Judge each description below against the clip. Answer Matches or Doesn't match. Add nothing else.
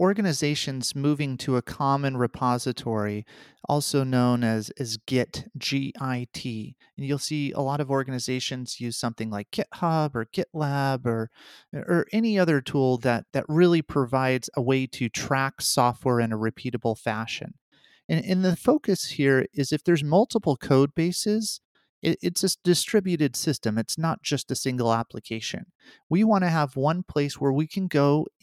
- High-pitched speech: Doesn't match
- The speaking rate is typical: Matches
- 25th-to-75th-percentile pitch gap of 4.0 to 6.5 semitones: Matches